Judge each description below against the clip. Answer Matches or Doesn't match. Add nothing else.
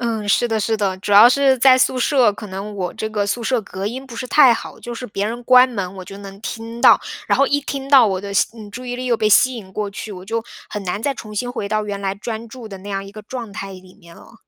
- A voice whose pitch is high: Matches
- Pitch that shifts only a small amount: Doesn't match